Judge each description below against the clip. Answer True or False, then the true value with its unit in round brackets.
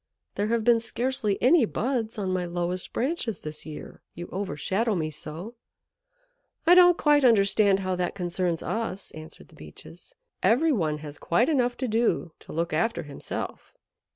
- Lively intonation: True (5.7 semitones)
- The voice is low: False (200 Hz)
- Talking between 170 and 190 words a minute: False (160 wpm)